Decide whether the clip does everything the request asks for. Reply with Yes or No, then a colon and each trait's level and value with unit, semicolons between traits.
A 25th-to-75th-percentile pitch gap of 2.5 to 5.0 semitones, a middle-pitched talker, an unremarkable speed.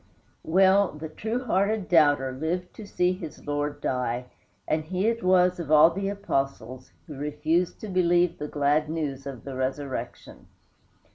Yes: average, 4.3 semitones; medium, 160 Hz; average, 155 wpm